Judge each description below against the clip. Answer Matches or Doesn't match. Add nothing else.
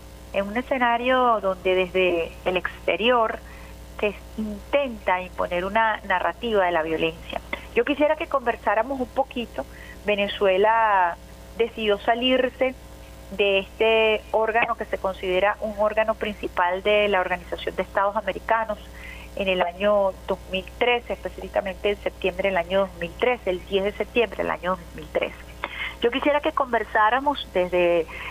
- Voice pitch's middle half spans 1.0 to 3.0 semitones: Doesn't match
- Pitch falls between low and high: Doesn't match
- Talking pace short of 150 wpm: Matches